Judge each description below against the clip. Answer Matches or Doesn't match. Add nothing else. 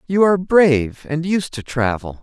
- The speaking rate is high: Doesn't match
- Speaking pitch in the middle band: Matches